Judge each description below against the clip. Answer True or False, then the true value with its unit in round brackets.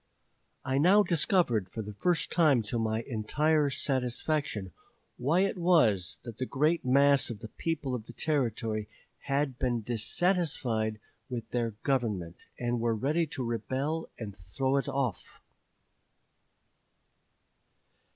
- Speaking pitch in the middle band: False (130 Hz)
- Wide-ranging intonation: False (5.0 semitones)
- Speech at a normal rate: False (130 wpm)